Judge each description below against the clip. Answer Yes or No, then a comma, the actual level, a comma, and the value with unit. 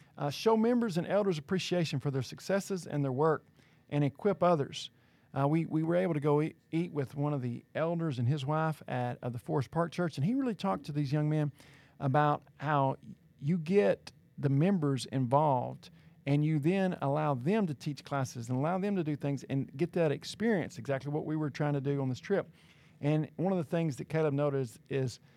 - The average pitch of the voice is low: No, medium, 150 Hz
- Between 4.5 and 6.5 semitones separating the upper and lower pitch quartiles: No, average, 3.5 semitones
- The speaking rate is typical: No, fast, 215 wpm